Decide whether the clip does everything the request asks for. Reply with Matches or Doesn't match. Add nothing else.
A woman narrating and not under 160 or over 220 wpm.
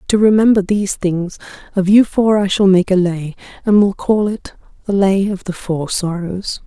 Matches